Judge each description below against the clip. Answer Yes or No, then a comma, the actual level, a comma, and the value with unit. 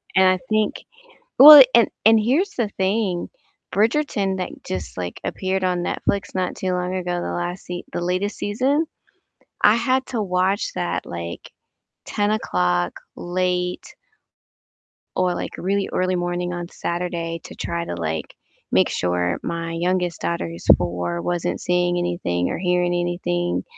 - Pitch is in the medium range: Yes, medium, 180 Hz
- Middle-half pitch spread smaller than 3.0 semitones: Yes, narrow, 2.6 semitones